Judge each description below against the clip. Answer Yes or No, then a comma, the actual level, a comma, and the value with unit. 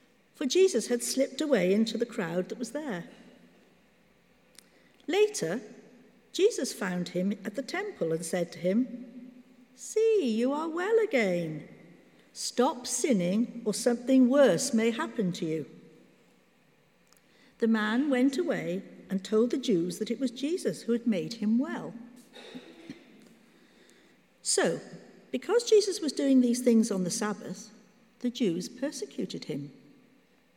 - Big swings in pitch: No, average, 3.9 semitones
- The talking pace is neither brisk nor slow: No, slow, 130 wpm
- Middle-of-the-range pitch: No, high, 240 Hz